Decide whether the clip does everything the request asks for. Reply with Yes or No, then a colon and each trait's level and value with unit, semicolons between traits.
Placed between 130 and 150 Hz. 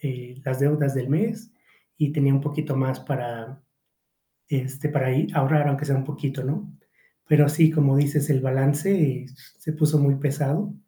Yes: medium, 140 Hz